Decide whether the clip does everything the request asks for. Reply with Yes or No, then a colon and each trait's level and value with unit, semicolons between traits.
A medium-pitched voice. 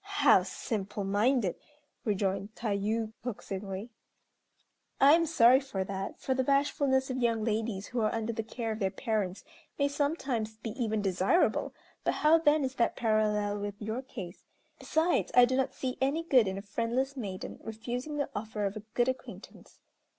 No: high, 230 Hz